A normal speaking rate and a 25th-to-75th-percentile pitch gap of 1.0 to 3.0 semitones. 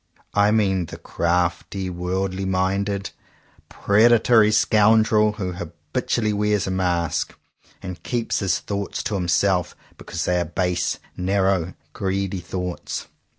No: slow, 120 wpm; average, 2.7 semitones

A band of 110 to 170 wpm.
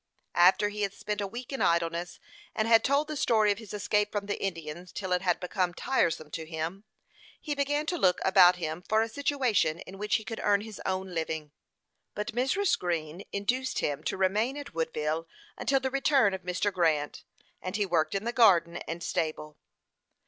No: average, 195 wpm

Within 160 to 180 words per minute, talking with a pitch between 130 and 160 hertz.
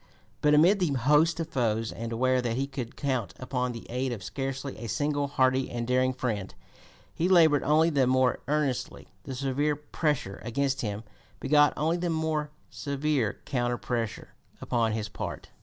Yes: average, 170 wpm; low, 135 Hz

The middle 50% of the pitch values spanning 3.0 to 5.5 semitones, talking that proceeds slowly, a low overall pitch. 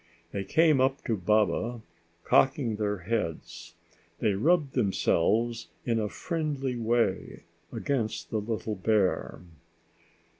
Yes: average, 4.1 semitones; slow, 110 wpm; low, 115 Hz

